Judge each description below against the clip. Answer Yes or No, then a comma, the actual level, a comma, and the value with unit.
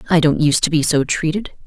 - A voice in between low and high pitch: Yes, medium, 160 Hz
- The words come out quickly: Yes, fast, 250 wpm